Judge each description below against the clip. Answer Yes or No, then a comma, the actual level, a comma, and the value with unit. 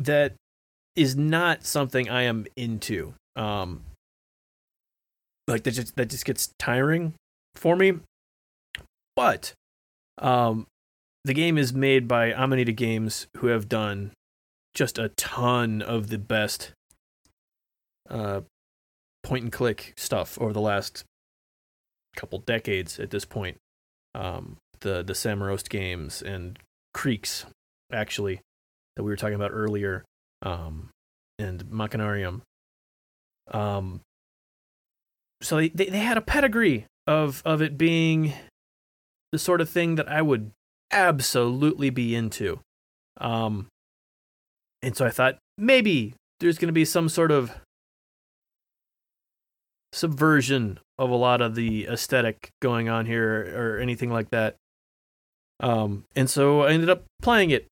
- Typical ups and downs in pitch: No, wide, 6.4 semitones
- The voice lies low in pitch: Yes, low, 115 Hz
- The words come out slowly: Yes, slow, 130 wpm